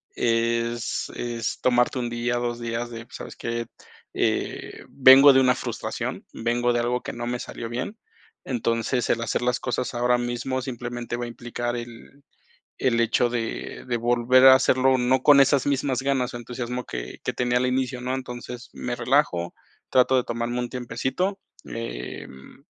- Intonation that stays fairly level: Yes, narrow, 1.4 semitones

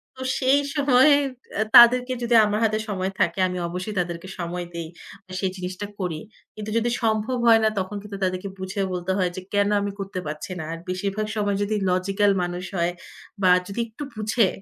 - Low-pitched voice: No, high, 200 Hz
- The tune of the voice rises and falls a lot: No, average, 3.0 semitones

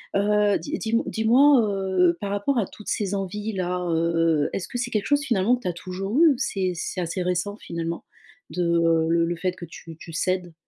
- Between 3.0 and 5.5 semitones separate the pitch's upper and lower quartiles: Yes, average, 3.6 semitones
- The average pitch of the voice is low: No, high, 190 Hz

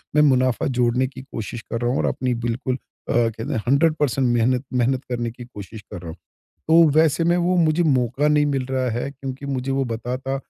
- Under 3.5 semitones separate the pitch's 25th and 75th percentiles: Yes, average, 2.7 semitones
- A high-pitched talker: No, low, 130 Hz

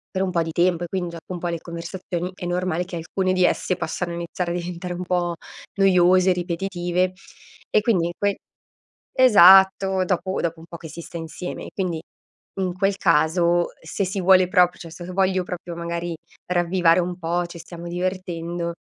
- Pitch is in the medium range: Yes, medium, 175 Hz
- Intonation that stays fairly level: Yes, narrow, 1.4 semitones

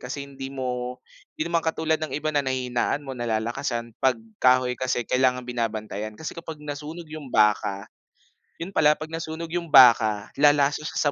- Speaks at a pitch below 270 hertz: Yes, low, 135 Hz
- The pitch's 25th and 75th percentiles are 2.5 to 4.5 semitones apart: Yes, average, 4.1 semitones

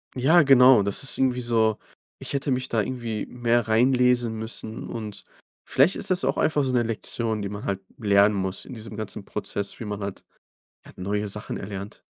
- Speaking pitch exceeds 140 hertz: No, low, 115 Hz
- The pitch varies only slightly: No, average, 3.3 semitones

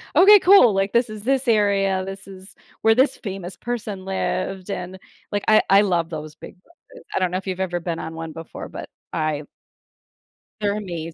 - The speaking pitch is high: Yes, high, 195 Hz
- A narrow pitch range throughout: No, average, 3.3 semitones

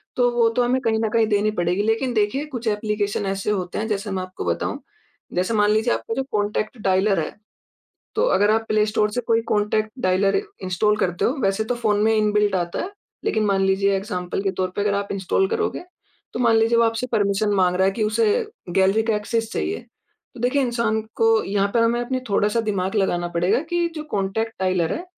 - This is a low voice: No, high, 210 Hz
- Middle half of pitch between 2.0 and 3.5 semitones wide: Yes, average, 2.8 semitones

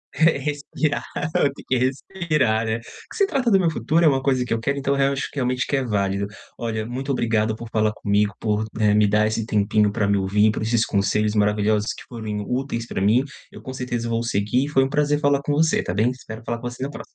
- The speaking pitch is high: No, low, 115 Hz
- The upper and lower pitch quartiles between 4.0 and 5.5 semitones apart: Yes, average, 4.4 semitones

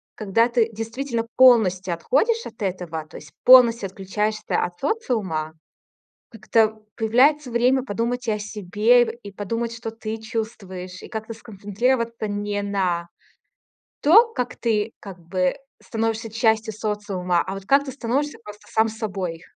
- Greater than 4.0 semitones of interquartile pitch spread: No, average, 3.2 semitones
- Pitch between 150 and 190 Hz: No, high, 220 Hz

